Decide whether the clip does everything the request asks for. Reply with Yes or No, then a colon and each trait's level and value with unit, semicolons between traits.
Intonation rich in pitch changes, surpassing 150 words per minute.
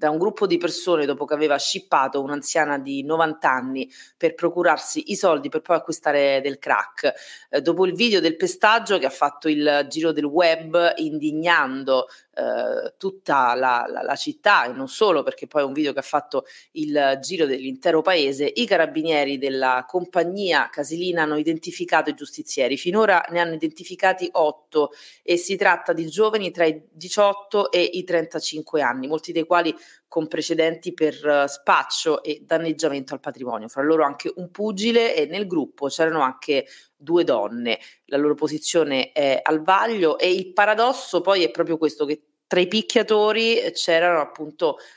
No: average, 3.9 semitones; fast, 170 wpm